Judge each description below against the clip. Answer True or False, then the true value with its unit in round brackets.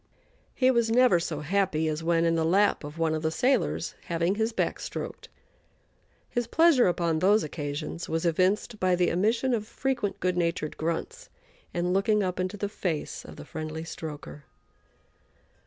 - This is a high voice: False (180 Hz)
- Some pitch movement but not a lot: True (4.8 semitones)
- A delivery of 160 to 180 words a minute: True (170 wpm)